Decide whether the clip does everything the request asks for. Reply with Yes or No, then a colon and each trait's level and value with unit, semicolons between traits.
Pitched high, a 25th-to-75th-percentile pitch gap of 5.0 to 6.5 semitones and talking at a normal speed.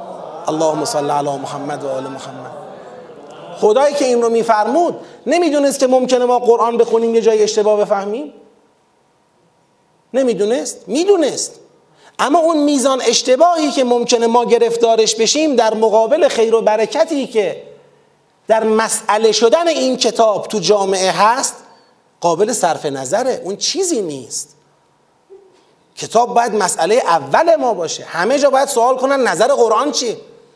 Yes: high, 235 Hz; wide, 5.4 semitones; average, 130 wpm